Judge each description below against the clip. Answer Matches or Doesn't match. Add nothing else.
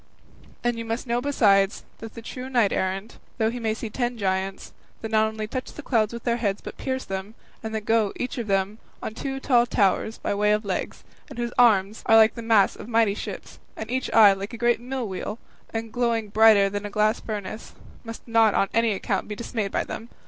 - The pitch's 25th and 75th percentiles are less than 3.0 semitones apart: Matches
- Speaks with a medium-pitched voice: Doesn't match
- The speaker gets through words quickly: Matches